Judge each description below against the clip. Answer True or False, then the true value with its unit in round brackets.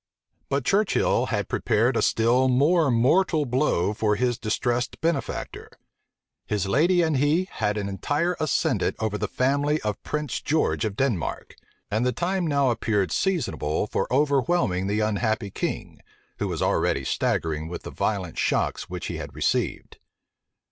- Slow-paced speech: False (150 wpm)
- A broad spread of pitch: True (6.3 semitones)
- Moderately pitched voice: False (125 Hz)